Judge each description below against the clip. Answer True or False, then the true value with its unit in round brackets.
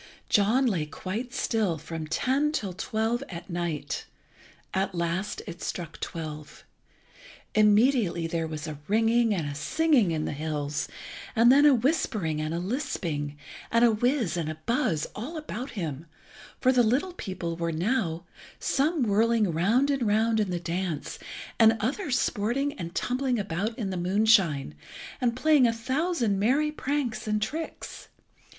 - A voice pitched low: False (210 Hz)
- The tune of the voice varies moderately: False (6.8 semitones)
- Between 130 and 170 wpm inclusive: True (155 wpm)